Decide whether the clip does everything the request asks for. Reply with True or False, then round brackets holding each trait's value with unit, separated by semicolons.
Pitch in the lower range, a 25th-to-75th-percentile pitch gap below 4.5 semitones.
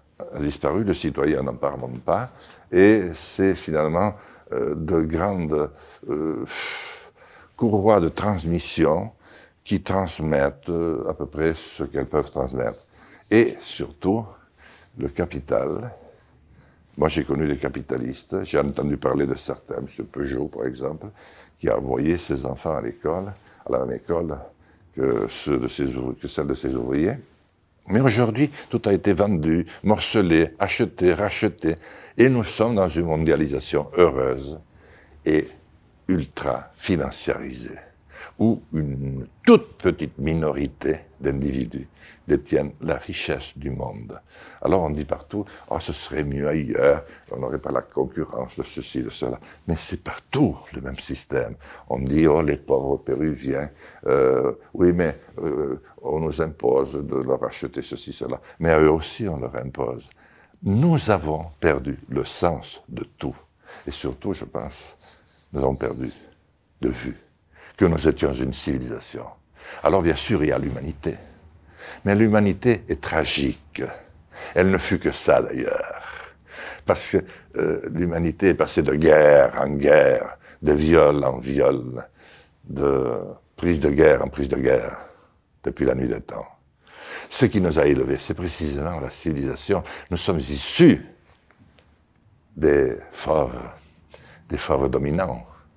False (80 Hz; 5.3 semitones)